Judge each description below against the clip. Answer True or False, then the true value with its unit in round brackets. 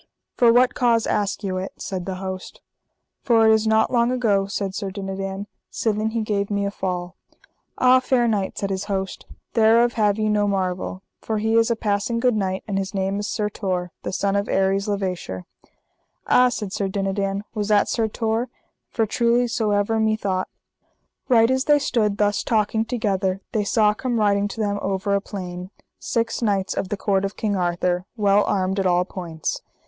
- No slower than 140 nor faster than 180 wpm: False (195 wpm)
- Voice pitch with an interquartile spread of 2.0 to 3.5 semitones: True (2.5 semitones)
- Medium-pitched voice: False (205 Hz)